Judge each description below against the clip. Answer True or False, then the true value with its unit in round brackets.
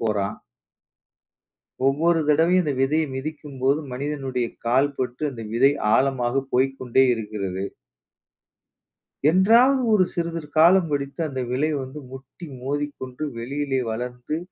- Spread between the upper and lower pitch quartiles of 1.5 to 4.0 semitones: True (3.6 semitones)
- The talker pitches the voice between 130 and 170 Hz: True (135 Hz)